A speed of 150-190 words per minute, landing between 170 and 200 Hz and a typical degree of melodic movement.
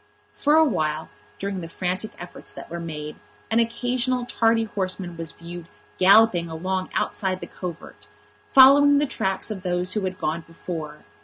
Yes: average, 160 wpm; medium, 185 Hz; average, 5.0 semitones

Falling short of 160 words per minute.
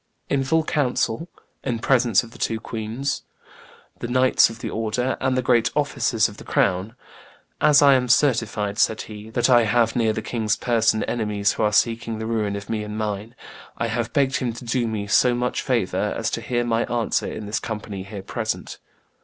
No: average, 200 wpm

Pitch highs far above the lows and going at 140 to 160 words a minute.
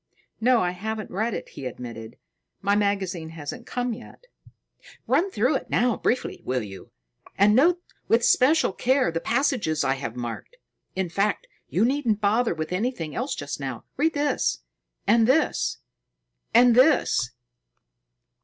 Yes: wide, 7.7 semitones; average, 145 wpm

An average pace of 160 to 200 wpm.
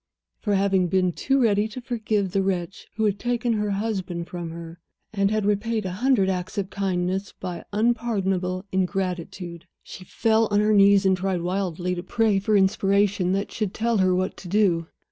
Yes: average, 185 wpm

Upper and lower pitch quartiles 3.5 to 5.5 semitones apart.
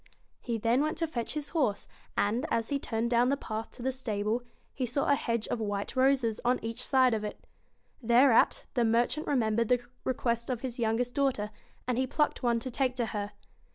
No: narrow, 2.6 semitones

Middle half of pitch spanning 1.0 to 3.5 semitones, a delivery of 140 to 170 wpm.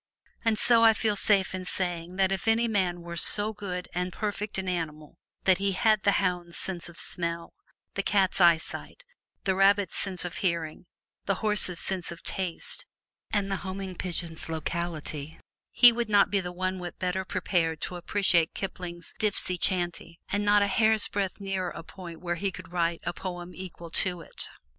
No: narrow, 2.5 semitones; average, 180 wpm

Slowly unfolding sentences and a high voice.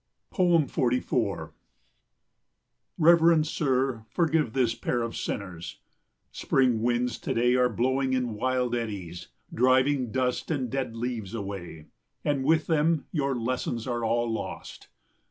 No: slow, 120 wpm; low, 125 Hz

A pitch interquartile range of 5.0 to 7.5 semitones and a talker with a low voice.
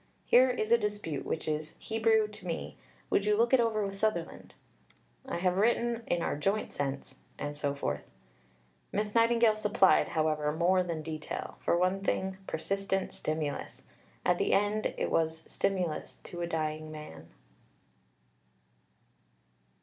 No: wide, 5.4 semitones; medium, 185 Hz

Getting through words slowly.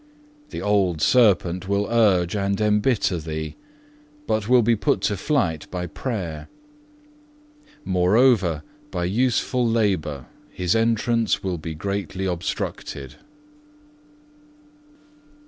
Yes: slow, 100 wpm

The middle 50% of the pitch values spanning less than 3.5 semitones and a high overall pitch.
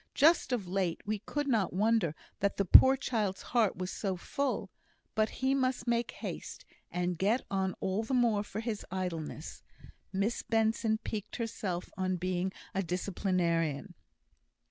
No: average, 4.0 semitones; high, 200 Hz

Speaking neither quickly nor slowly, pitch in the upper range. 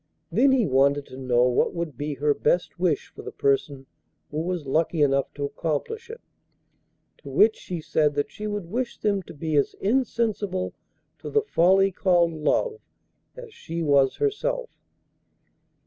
No: average, 165 wpm; medium, 170 Hz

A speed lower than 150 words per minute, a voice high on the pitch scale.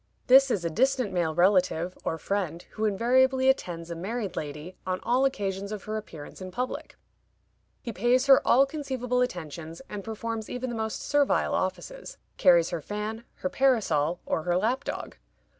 No: average, 165 wpm; high, 210 Hz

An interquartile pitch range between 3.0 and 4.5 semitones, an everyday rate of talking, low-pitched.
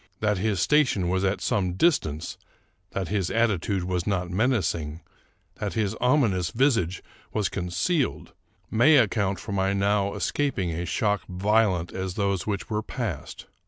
Yes: average, 3.5 semitones; average, 150 wpm; low, 100 Hz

